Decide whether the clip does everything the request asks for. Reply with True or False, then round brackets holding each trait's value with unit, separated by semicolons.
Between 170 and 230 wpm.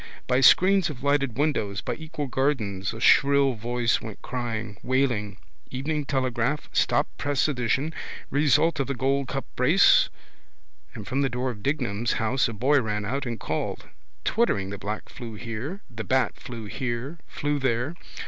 False (150 wpm)